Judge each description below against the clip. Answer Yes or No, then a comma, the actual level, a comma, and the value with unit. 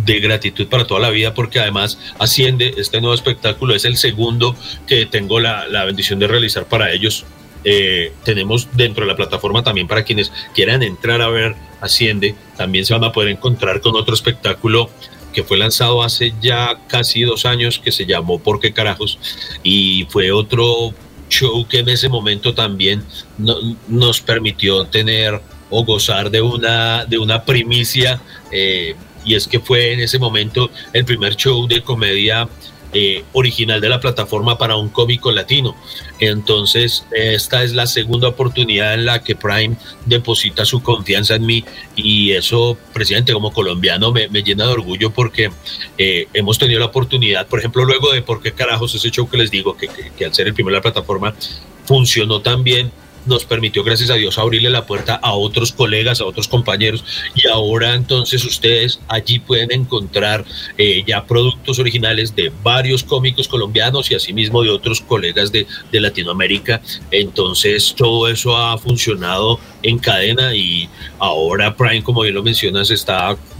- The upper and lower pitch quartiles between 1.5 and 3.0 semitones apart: Yes, narrow, 2.4 semitones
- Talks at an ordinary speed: Yes, average, 170 wpm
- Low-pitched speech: Yes, low, 115 Hz